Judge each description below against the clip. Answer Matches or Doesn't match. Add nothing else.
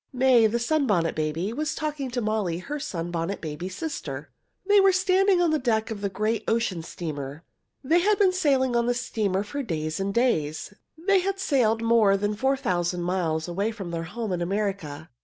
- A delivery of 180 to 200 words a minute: Matches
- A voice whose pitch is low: Doesn't match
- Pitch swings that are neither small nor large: Doesn't match